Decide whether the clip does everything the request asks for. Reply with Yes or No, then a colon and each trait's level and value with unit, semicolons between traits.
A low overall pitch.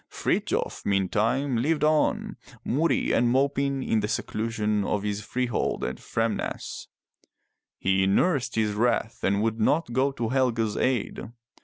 Yes: low, 115 Hz